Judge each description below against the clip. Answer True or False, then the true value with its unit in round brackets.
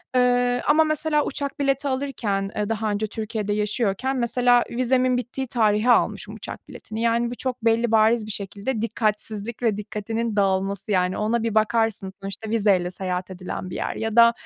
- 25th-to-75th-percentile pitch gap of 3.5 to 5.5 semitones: False (3.1 semitones)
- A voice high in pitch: True (225 Hz)